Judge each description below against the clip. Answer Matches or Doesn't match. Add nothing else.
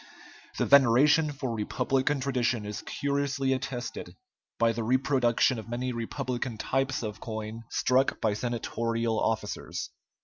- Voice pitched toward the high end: Doesn't match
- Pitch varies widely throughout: Doesn't match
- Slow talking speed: Matches